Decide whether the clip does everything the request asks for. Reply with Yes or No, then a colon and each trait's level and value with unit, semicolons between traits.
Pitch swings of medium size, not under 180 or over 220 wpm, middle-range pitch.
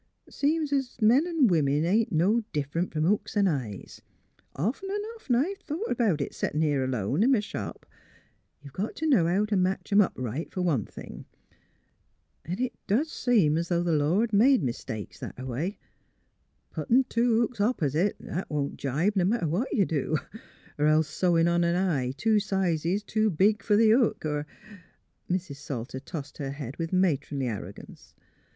No: wide, 6.9 semitones; average, 190 wpm; medium, 180 Hz